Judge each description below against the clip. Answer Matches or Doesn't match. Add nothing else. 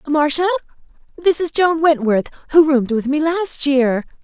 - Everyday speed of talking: Matches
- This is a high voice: Matches